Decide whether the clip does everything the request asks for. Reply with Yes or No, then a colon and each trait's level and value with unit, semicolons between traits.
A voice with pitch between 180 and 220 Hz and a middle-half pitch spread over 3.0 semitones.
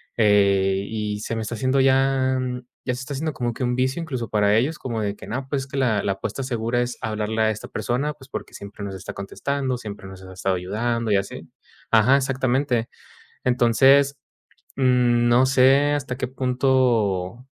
No: low, 120 Hz; average, 3.8 semitones